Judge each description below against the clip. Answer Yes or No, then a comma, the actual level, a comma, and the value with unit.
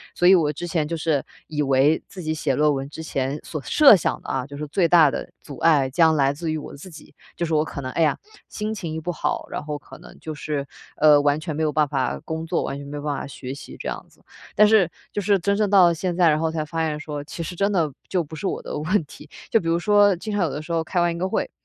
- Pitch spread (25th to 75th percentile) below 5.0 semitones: Yes, average, 3.0 semitones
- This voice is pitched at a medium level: Yes, medium, 155 Hz